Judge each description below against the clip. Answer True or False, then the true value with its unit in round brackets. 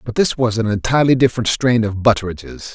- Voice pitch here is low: True (115 Hz)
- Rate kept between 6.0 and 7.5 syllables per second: True (6.4 syllables/s)